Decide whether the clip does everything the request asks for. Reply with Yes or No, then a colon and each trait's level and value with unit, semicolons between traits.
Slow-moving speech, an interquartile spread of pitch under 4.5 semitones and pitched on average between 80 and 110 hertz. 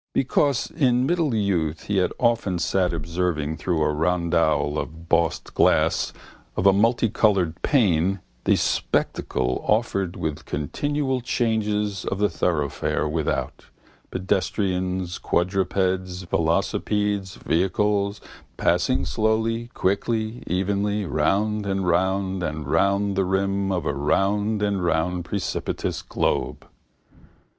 Yes: slow, 110 wpm; average, 3.5 semitones; very low, 95 Hz